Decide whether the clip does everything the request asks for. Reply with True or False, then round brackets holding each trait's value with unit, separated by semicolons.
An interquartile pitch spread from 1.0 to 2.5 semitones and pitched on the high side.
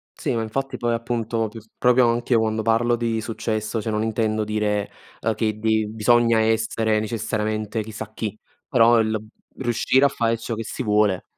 False (1.4 semitones; 110 Hz)